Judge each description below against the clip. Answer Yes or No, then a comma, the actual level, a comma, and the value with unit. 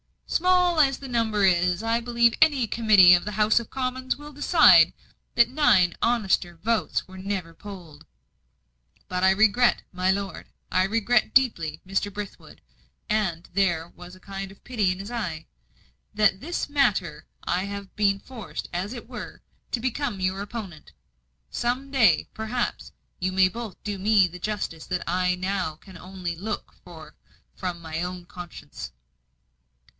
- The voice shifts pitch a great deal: No, average, 4.5 semitones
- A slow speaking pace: No, average, 160 wpm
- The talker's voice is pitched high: Yes, high, 200 Hz